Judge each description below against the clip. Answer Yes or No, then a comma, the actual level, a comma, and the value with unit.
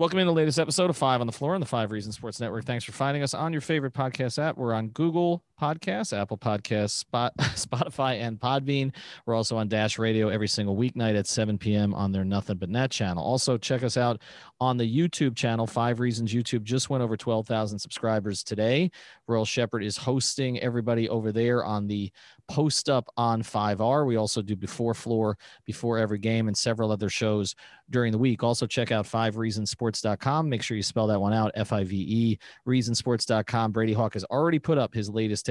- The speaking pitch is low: Yes, low, 115 Hz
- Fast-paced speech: Yes, fast, 210 wpm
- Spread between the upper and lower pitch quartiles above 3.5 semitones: No, average, 3.2 semitones